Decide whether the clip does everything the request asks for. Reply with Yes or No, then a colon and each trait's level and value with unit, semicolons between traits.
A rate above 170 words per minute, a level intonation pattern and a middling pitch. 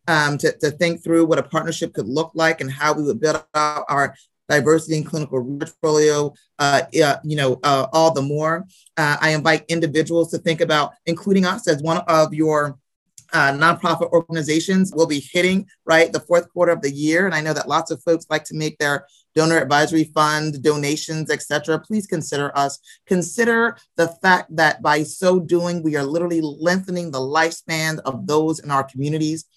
Yes: average, 190 wpm; narrow, 2.0 semitones; medium, 160 Hz